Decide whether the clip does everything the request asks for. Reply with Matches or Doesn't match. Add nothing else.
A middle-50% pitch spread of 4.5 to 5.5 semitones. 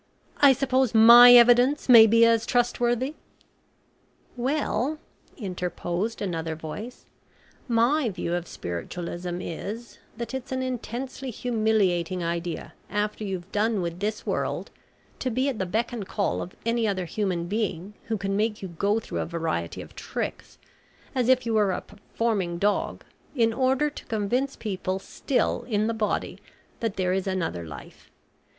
Matches